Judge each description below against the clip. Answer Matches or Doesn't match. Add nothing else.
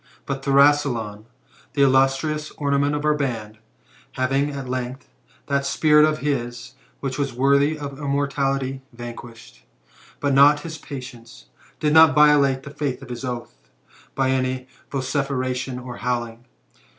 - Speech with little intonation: Matches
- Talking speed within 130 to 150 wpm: Matches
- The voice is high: Doesn't match